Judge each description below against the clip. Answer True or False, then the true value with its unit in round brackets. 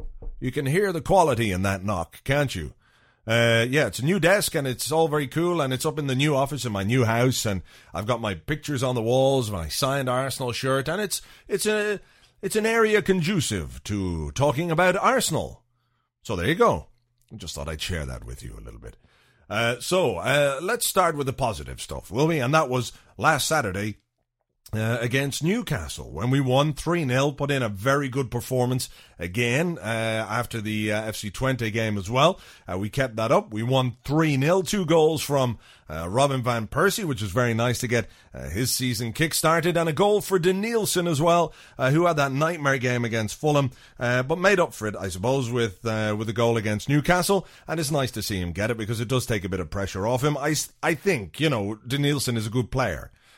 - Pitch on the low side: True (130 Hz)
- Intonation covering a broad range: True (5.8 semitones)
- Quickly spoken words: True (215 wpm)